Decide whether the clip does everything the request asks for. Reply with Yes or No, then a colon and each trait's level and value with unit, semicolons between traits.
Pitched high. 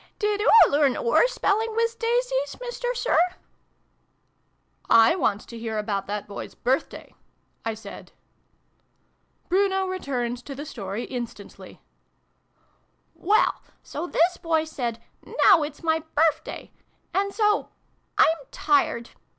Yes: very high, 320 Hz